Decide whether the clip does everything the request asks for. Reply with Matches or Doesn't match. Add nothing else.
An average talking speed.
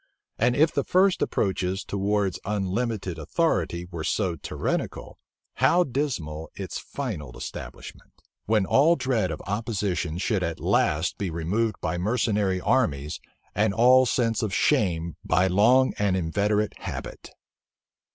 Doesn't match